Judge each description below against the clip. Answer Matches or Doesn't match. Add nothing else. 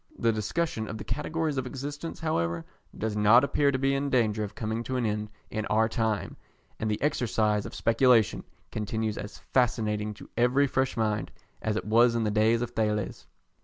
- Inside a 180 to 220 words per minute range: Matches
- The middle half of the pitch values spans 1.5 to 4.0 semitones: Matches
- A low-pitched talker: Matches